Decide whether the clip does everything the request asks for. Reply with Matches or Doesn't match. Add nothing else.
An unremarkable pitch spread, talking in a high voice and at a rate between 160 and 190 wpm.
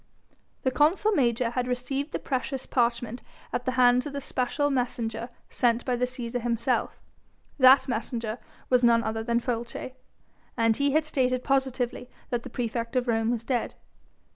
Doesn't match